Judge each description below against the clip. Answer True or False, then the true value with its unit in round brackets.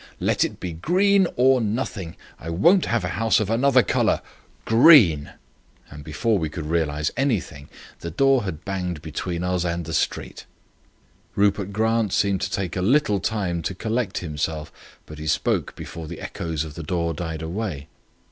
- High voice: False (90 Hz)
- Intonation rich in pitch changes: True (5.7 semitones)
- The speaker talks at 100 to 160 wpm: False (170 wpm)